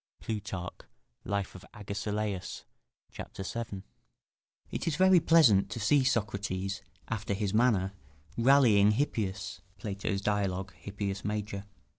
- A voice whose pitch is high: No, low, 105 Hz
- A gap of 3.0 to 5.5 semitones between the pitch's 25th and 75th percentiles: No, narrow, 2.5 semitones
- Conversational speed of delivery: No, slow, 110 wpm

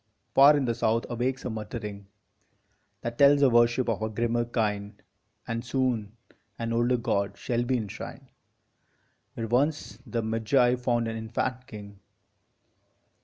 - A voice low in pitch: Yes, low, 115 Hz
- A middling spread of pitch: No, narrow, 2.2 semitones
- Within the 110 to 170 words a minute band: Yes, average, 140 wpm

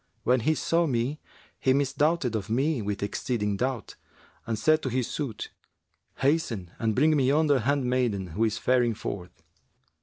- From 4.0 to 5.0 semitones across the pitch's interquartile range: Yes, average, 4.5 semitones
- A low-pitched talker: Yes, low, 125 Hz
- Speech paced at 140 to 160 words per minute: Yes, average, 155 wpm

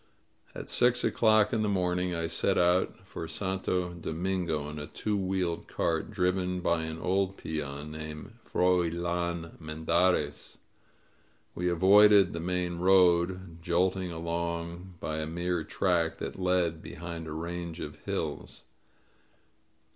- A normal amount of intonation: No, narrow, 2.1 semitones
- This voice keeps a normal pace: No, slow, 130 wpm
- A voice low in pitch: Yes, very low, 85 Hz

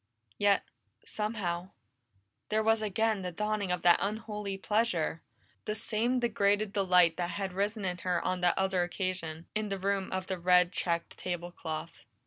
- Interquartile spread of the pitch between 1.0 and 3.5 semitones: Yes, average, 3.0 semitones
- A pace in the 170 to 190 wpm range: No, average, 160 wpm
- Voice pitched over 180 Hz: Yes, high, 190 Hz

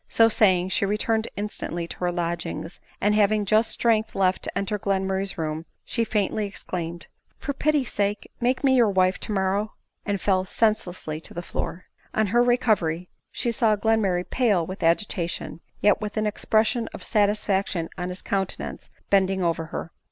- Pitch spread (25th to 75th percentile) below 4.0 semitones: Yes, average, 3.1 semitones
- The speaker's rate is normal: Yes, average, 180 wpm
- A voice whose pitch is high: Yes, high, 200 Hz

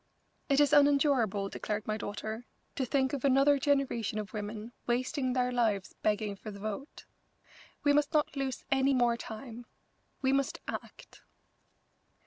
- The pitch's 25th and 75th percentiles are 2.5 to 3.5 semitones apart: No, average, 4.3 semitones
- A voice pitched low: No, very high, 250 Hz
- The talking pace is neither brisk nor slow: Yes, average, 145 wpm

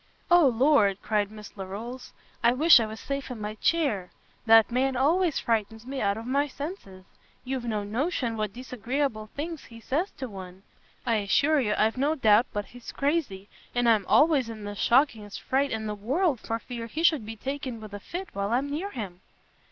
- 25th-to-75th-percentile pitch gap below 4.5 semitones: No, average, 4.8 semitones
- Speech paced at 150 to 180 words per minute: No, average, 195 wpm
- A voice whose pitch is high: Yes, high, 235 Hz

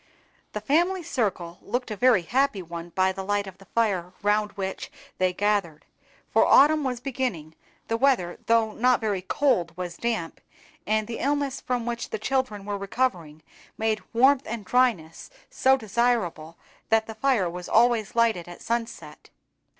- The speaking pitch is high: Yes, high, 220 Hz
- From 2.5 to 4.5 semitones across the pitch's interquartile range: No, average, 5.0 semitones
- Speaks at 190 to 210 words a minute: No, average, 160 wpm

